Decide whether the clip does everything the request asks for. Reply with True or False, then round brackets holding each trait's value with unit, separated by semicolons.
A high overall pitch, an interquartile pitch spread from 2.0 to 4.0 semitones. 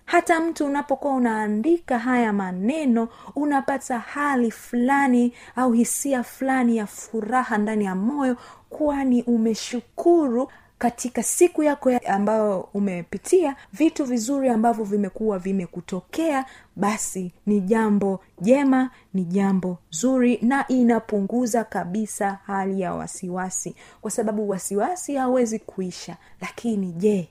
False (235 Hz; 4.7 semitones)